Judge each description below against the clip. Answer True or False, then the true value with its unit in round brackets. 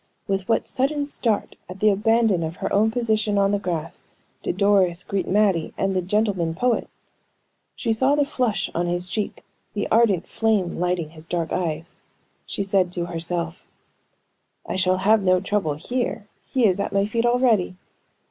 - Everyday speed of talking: True (175 wpm)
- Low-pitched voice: False (195 Hz)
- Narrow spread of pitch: False (3.7 semitones)